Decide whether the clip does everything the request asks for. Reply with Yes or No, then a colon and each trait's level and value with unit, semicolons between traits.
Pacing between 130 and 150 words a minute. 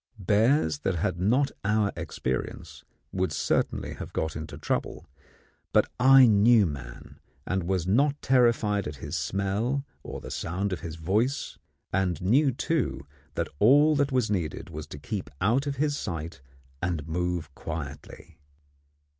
Yes: average, 145 wpm